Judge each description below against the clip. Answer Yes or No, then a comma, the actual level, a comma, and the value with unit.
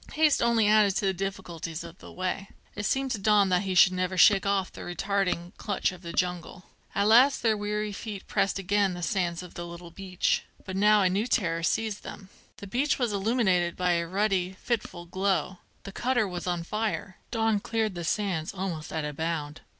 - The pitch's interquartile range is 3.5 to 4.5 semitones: No, average, 3.0 semitones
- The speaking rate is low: No, average, 200 wpm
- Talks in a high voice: Yes, high, 195 Hz